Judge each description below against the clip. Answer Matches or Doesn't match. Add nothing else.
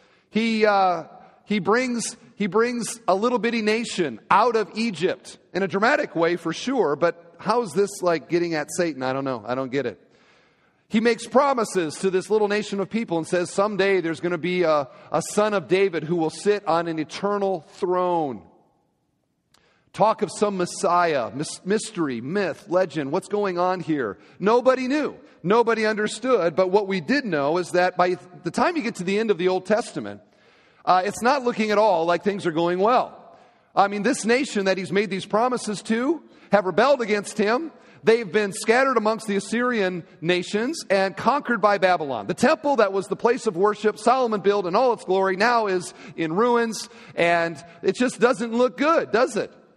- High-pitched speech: Matches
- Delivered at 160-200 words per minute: Matches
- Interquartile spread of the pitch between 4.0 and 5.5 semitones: Matches